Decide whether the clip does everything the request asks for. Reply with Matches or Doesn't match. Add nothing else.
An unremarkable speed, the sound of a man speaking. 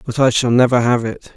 Doesn't match